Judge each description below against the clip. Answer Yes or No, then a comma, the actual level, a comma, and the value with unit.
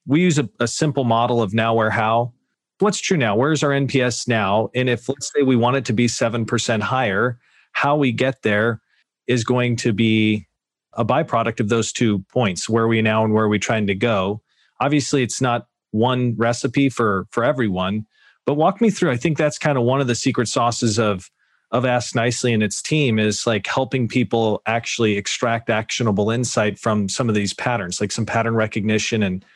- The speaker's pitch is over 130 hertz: No, low, 115 Hz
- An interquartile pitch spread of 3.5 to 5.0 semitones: No, average, 2.7 semitones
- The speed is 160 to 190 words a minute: No, fast, 205 wpm